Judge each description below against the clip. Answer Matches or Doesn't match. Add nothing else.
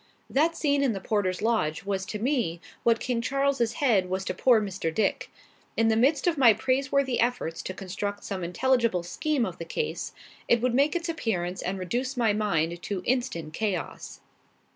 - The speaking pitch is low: Doesn't match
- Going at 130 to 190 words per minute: Matches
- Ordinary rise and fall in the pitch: Doesn't match